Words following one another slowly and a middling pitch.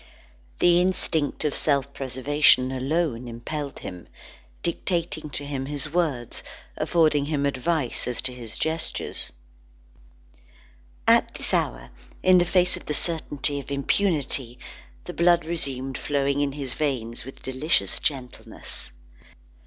Yes: slow, 125 wpm; medium, 145 Hz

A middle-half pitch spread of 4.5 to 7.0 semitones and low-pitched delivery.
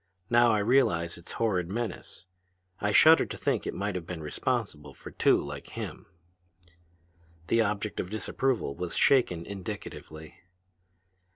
Yes: average, 5.3 semitones; low, 100 Hz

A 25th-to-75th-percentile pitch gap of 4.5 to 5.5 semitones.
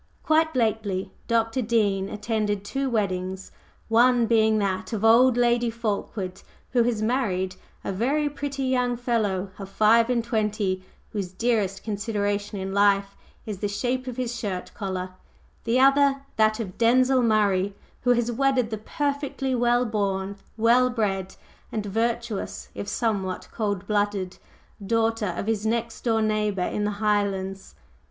No: average, 3.2 semitones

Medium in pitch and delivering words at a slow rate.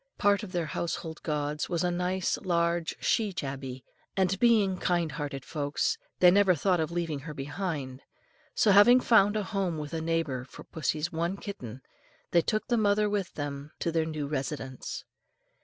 No: medium, 170 Hz; average, 175 wpm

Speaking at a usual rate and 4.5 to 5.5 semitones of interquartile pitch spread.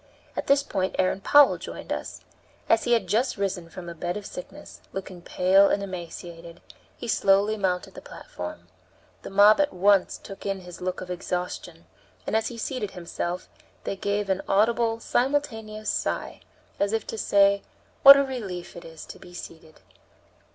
No: average, 170 wpm; average, 3.6 semitones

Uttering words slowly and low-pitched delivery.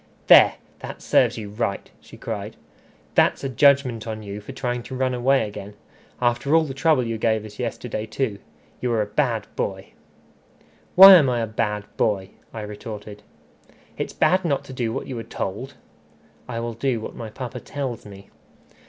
No: average, 180 wpm; low, 115 Hz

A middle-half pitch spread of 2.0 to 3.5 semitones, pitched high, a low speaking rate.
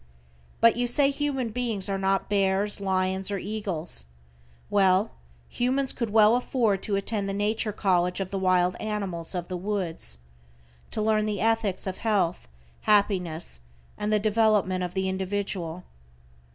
No: narrow, 2.6 semitones; high, 200 Hz; average, 150 wpm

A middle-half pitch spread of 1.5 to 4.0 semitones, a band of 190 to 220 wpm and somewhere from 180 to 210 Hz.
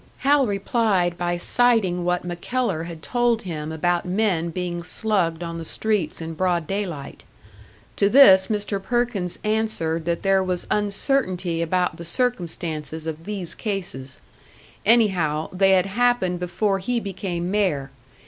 No: average, 3.7 semitones; average, 140 wpm; medium, 185 Hz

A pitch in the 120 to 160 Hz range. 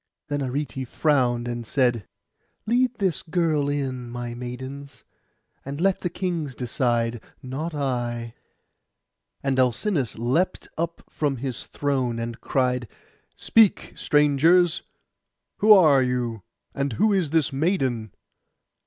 Yes: low, 135 Hz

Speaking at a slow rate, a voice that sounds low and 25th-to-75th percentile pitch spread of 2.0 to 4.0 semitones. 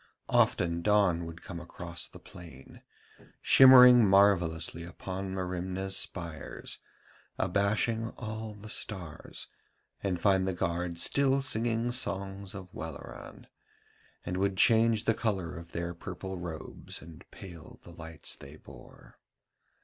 Yes: slow, 120 wpm; very low, 95 Hz; average, 3.6 semitones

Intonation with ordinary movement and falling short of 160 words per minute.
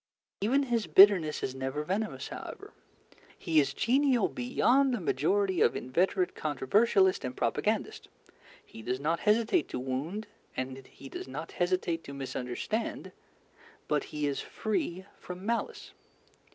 No: wide, 7.6 semitones; slow, 135 wpm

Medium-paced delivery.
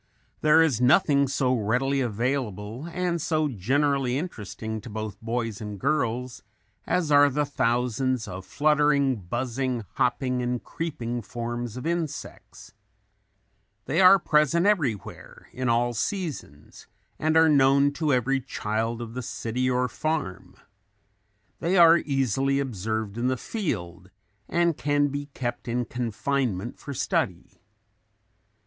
No: slow, 130 wpm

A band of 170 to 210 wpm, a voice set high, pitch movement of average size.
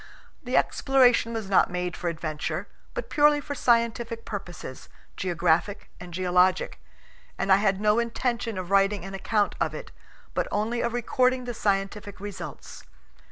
No: average, 150 wpm; high, 205 Hz; average, 4.2 semitones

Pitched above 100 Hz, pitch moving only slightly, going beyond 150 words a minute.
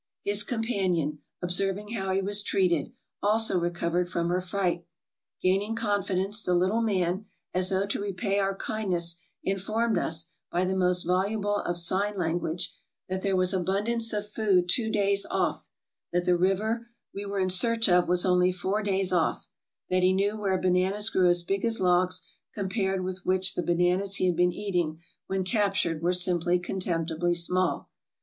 Yes: medium, 185 Hz; narrow, 2.3 semitones; average, 170 wpm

